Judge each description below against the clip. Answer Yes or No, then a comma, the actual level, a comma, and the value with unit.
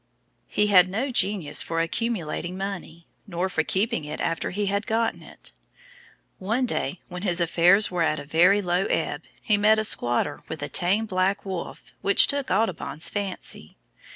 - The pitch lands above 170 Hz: Yes, high, 190 Hz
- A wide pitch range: No, average, 3.5 semitones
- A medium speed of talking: Yes, average, 170 wpm